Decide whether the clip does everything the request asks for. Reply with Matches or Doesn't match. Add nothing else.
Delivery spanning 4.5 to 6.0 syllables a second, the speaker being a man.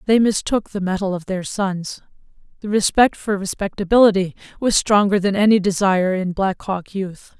Doesn't match